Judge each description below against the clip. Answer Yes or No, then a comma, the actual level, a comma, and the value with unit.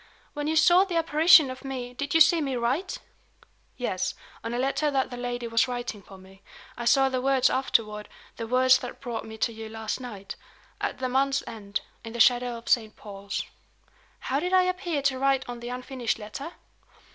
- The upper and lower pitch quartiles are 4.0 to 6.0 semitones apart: No, average, 3.3 semitones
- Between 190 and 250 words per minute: Yes, average, 200 wpm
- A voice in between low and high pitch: No, very high, 250 Hz